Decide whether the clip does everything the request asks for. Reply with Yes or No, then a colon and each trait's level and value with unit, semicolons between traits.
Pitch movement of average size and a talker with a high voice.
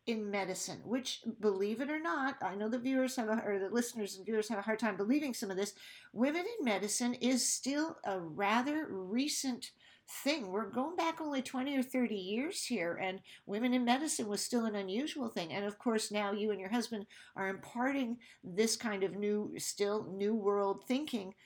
Yes: average, 4.0 semitones; high, 225 Hz